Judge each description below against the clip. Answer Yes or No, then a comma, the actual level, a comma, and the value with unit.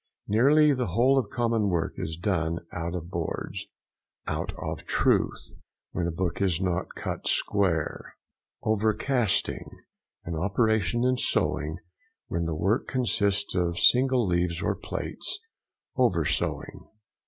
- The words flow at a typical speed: No, slow, 120 wpm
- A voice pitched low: Yes, very low, 95 Hz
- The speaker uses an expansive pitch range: Yes, wide, 5.7 semitones